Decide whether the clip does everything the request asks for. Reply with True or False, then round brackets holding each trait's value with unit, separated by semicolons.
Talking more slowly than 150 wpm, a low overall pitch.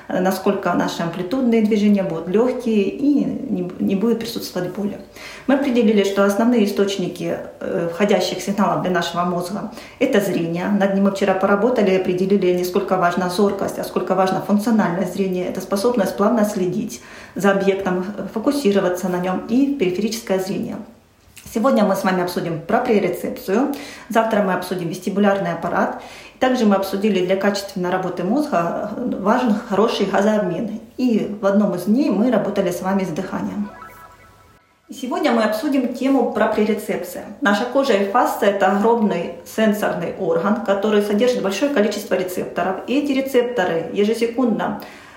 False (140 wpm; 205 Hz)